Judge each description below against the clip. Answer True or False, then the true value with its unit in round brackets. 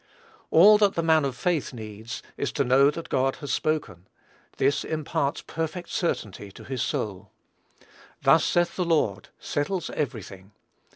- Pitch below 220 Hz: True (140 Hz)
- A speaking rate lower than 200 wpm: True (155 wpm)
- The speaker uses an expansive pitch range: True (6.7 semitones)